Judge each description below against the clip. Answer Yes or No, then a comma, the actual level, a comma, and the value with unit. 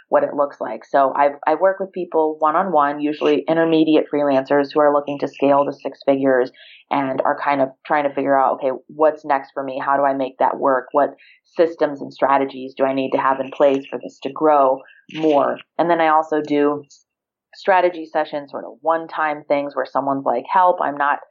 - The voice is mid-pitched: Yes, medium, 145 Hz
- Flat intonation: Yes, narrow, 2.2 semitones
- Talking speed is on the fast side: Yes, fast, 215 wpm